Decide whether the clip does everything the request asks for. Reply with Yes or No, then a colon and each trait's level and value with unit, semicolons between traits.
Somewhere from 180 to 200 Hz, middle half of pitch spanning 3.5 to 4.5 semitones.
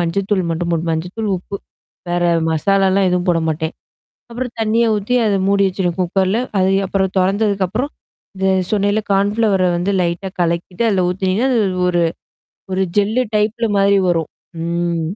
No: high, 190 Hz; average, 2.8 semitones